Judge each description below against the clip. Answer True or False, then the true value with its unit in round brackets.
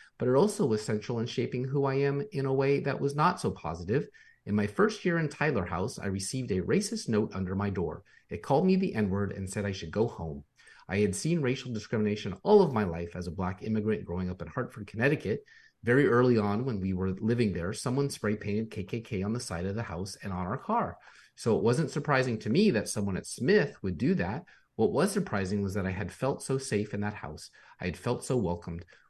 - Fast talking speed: True (240 wpm)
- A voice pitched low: True (110 Hz)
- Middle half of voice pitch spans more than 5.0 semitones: True (5.5 semitones)